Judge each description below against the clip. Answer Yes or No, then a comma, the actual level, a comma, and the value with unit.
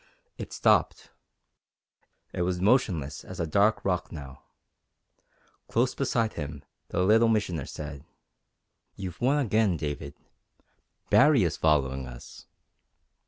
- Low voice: Yes, very low, 90 Hz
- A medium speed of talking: No, slow, 115 wpm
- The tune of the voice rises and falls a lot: Yes, wide, 7.1 semitones